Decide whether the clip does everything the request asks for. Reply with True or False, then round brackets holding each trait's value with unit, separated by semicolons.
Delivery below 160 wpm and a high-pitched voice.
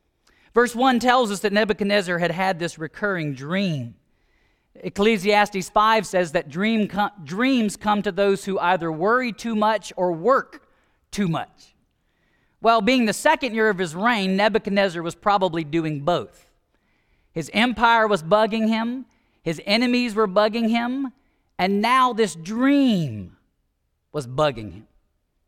True (140 wpm; 205 Hz)